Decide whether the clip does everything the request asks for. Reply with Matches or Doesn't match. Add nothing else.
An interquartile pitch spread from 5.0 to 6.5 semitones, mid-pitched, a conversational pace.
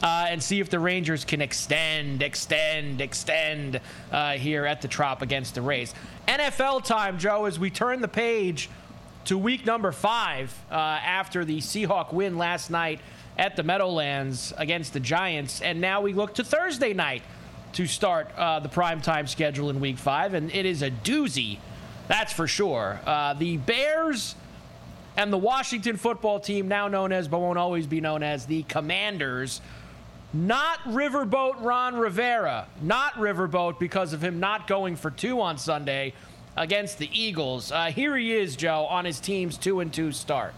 Matches